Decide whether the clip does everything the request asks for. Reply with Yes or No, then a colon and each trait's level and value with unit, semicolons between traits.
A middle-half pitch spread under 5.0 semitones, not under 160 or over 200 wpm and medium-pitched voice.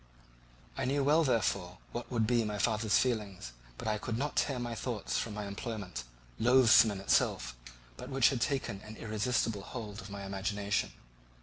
No: average, 3.4 semitones; average, 175 wpm; low, 110 Hz